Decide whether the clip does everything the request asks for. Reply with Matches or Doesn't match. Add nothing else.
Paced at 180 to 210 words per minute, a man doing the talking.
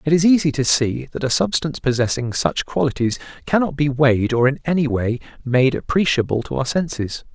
Matches